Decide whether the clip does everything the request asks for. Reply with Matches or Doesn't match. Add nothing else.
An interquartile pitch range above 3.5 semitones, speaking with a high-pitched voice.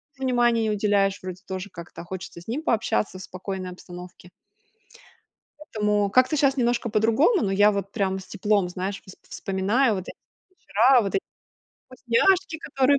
Matches